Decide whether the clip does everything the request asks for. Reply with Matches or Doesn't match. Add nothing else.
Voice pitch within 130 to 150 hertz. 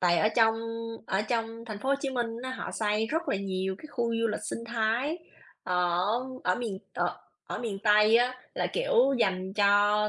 Doesn't match